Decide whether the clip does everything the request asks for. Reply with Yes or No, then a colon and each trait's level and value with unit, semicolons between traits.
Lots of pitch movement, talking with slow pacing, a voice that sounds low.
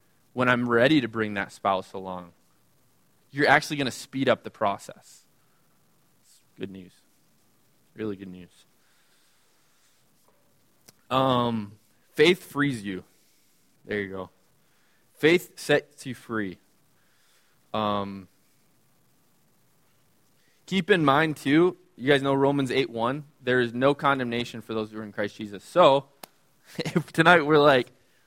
Yes: wide, 5.7 semitones; slow, 125 wpm; low, 120 Hz